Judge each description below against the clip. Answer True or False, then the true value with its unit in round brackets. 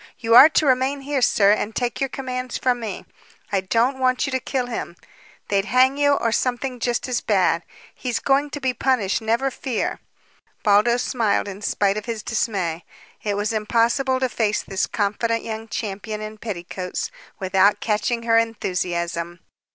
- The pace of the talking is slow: False (170 wpm)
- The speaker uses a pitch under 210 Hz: False (230 Hz)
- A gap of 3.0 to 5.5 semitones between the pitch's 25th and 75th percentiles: True (3.8 semitones)